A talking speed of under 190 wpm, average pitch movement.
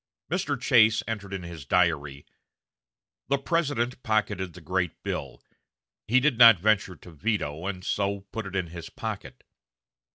Yes: average, 150 wpm; average, 4.4 semitones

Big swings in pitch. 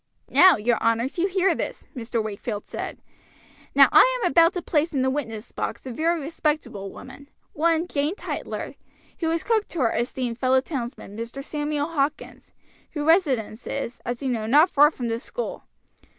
Yes: wide, 5.7 semitones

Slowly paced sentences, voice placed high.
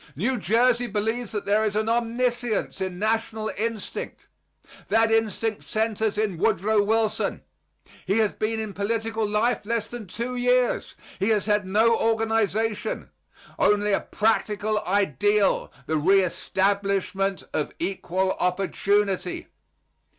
Yes: slow, 120 wpm; high, 215 Hz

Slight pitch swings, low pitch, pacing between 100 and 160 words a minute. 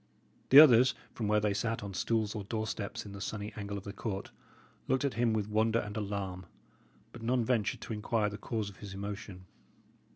No: narrow, 2.1 semitones; low, 105 Hz; average, 200 wpm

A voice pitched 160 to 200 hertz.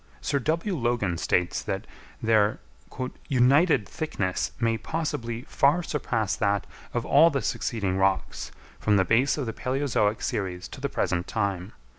No: low, 115 Hz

